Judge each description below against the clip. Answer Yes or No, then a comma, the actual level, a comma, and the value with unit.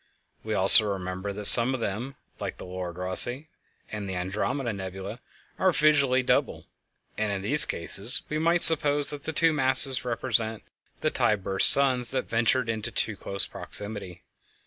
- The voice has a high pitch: No, low, 115 Hz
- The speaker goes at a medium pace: Yes, average, 165 wpm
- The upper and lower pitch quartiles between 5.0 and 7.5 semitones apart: Yes, wide, 5.5 semitones